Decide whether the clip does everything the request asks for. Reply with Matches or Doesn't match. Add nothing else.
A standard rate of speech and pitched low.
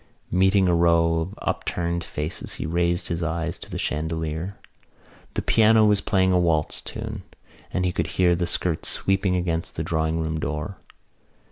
Matches